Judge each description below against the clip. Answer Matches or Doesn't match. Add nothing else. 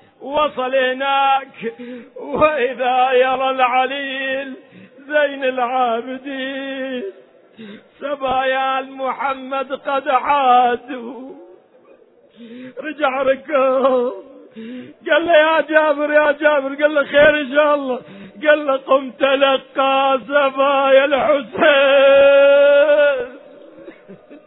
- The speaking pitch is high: Matches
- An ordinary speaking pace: Matches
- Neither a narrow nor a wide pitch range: Doesn't match